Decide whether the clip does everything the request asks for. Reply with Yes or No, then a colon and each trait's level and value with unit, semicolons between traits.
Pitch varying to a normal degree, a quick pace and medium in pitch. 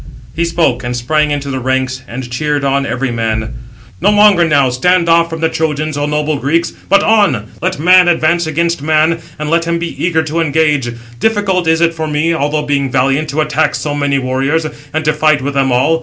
Yes: average, 3.4 semitones; fast, 210 wpm; medium, 155 Hz